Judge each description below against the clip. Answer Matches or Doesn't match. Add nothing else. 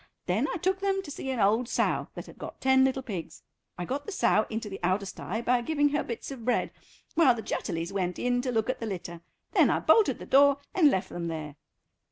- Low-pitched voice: Doesn't match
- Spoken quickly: Matches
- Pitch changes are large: Matches